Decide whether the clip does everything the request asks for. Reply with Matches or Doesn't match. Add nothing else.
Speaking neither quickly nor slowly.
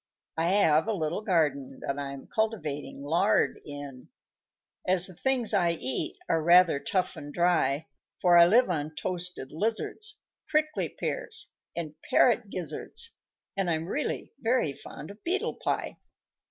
Matches